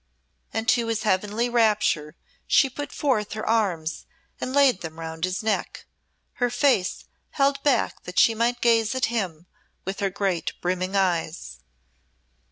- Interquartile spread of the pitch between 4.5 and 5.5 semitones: Yes, average, 4.8 semitones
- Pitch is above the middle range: Yes, high, 215 Hz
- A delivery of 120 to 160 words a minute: Yes, average, 150 wpm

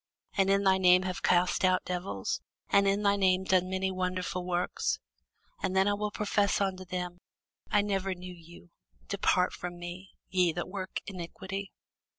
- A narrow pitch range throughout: Yes, narrow, 1.4 semitones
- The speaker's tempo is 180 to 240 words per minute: No, average, 165 wpm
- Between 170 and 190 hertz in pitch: Yes, medium, 185 Hz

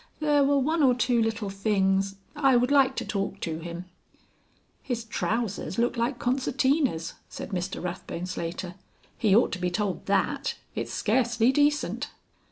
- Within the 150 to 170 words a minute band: Yes, average, 155 wpm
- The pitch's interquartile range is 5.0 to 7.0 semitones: Yes, wide, 5.5 semitones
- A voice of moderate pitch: No, high, 225 Hz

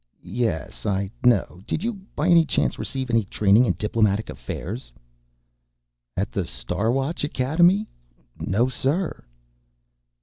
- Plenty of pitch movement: Yes, wide, 6.9 semitones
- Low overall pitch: Yes, low, 120 Hz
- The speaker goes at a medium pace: No, slow, 125 wpm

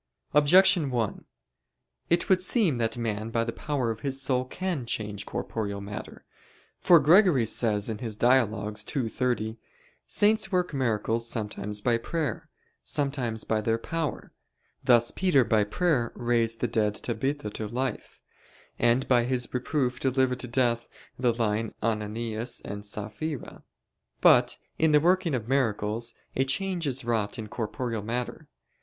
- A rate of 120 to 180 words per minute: Yes, average, 140 wpm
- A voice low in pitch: Yes, low, 120 Hz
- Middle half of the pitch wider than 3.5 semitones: Yes, average, 4.0 semitones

